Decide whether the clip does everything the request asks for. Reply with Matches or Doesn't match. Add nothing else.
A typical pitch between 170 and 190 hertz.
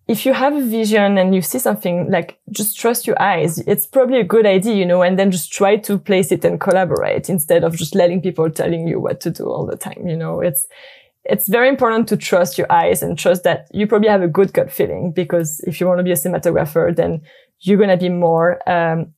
Matches